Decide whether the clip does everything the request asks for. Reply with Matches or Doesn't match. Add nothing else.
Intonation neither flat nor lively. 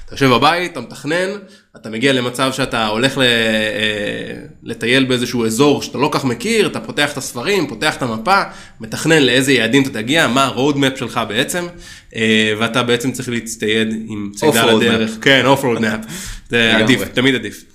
Matches